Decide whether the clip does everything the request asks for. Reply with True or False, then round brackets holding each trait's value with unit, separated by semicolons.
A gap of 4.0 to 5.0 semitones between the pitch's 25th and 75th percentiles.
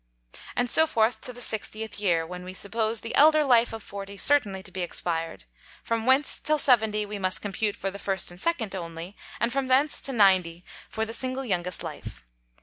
True (4.7 semitones)